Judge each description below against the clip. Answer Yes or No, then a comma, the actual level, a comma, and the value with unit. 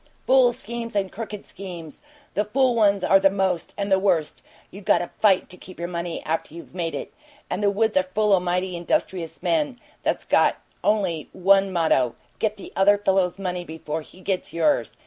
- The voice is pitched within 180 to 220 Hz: Yes, high, 190 Hz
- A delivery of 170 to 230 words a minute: Yes, average, 195 wpm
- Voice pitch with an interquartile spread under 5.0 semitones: Yes, average, 2.9 semitones